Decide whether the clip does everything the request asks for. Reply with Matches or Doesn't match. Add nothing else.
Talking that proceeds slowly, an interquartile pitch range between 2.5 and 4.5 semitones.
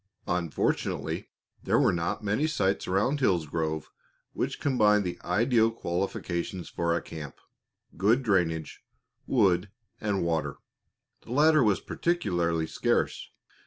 Doesn't match